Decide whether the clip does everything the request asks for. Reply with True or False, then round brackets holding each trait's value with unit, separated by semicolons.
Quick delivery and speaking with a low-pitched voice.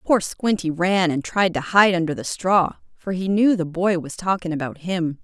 False (220 wpm; 180 Hz)